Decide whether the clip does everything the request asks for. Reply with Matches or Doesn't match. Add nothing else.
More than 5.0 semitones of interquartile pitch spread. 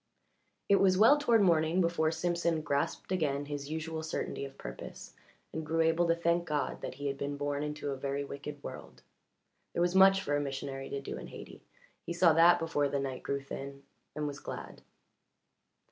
Doesn't match